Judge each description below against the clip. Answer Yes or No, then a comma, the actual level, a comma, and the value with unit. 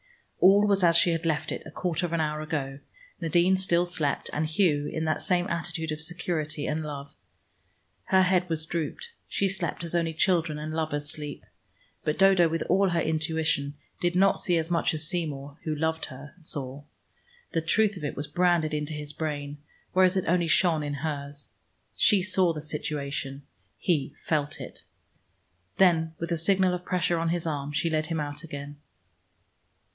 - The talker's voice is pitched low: No, medium, 160 Hz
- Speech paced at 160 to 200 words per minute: Yes, average, 180 wpm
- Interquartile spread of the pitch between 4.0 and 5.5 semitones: No, average, 2.8 semitones